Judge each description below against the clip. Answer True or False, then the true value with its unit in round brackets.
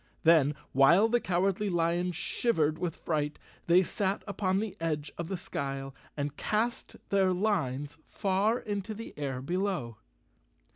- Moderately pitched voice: True (175 Hz)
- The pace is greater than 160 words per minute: False (140 wpm)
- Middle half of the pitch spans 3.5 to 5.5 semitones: True (5.1 semitones)